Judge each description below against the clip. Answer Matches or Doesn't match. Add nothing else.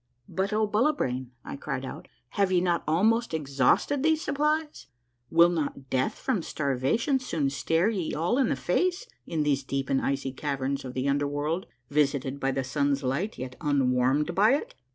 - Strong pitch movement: Matches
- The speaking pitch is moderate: Matches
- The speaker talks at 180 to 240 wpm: Matches